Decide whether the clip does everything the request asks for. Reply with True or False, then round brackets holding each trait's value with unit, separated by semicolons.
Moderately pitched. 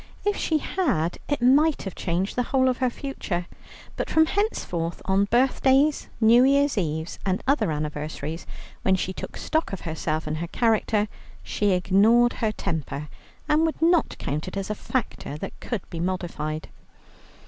False (205 Hz)